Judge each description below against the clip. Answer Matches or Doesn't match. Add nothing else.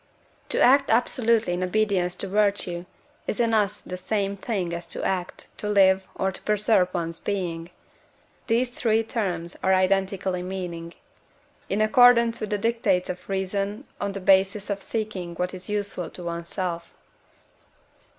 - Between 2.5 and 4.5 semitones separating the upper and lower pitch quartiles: Matches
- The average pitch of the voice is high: Matches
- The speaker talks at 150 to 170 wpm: Matches